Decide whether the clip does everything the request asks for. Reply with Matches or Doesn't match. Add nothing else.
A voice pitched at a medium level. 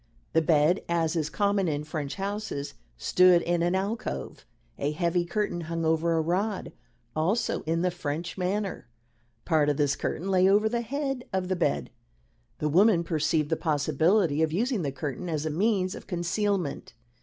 Matches